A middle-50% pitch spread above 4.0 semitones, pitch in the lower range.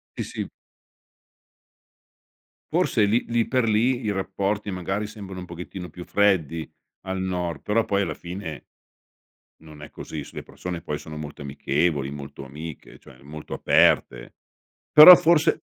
Yes: average, 5.1 semitones; very low, 90 Hz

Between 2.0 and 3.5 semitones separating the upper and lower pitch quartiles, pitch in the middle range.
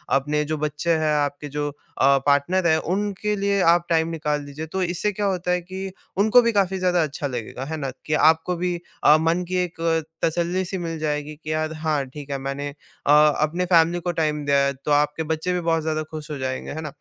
Yes: average, 3.2 semitones; medium, 160 Hz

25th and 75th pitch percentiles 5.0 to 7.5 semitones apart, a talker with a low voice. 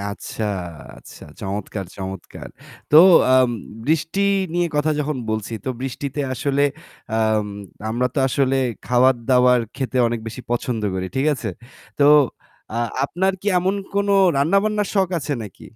Yes: average, 5.3 semitones; low, 130 Hz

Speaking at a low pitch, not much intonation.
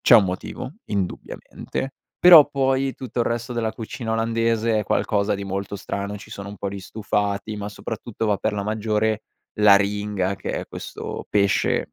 Yes: low, 105 Hz; narrow, 2.3 semitones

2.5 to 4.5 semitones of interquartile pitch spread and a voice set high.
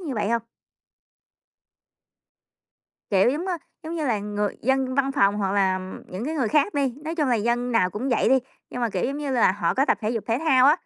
No: average, 5.2 semitones; high, 245 Hz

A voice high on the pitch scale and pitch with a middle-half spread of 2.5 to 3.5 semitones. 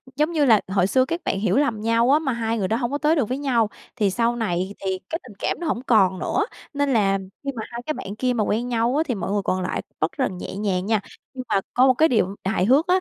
No: high, 230 Hz; average, 5.2 semitones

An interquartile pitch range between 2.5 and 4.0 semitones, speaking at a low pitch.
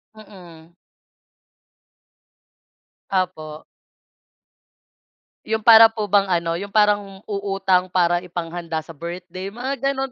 No: average, 3.4 semitones; medium, 185 Hz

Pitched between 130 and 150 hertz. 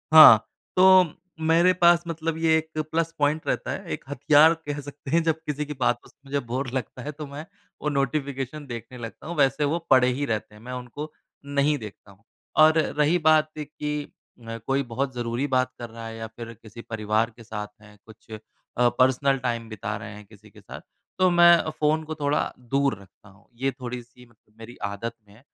Yes: low, 135 Hz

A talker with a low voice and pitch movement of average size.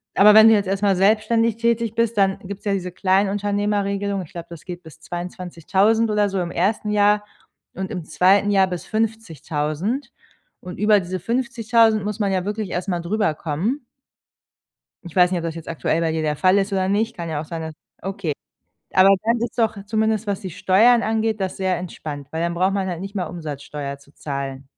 No: high, 195 Hz; average, 3.6 semitones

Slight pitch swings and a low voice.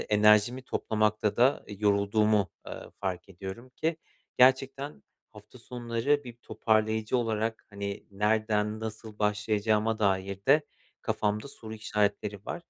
Yes: narrow, 2.1 semitones; low, 110 Hz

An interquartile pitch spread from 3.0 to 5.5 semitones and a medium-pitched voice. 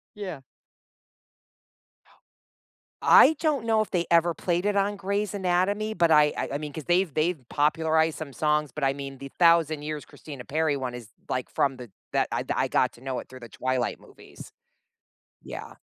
Yes: average, 4.8 semitones; medium, 155 Hz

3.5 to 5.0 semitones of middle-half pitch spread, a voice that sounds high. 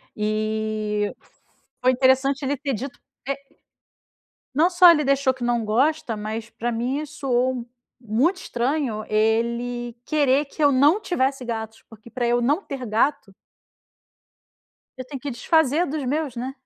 Yes: average, 3.8 semitones; very high, 255 Hz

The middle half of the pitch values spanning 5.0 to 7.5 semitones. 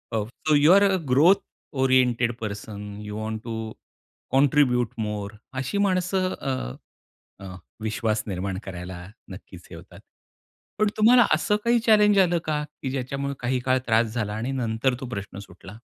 Yes: wide, 5.5 semitones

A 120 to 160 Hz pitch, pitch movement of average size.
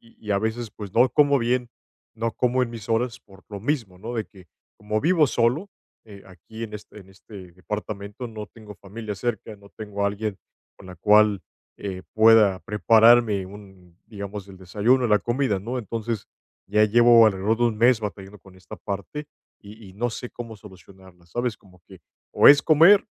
No: low, 105 Hz; average, 3.1 semitones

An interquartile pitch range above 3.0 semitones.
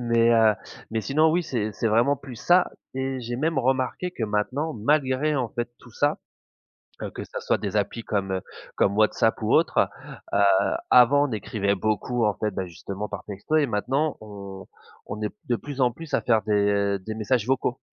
Yes: average, 4.2 semitones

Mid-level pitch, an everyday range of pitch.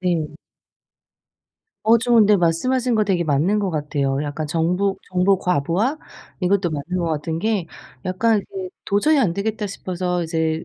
Yes: medium, 180 Hz; average, 4.3 semitones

